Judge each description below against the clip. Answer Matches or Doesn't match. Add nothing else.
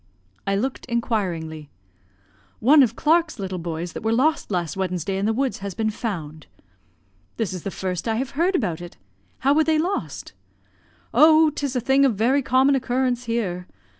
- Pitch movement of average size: Doesn't match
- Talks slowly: Doesn't match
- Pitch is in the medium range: Doesn't match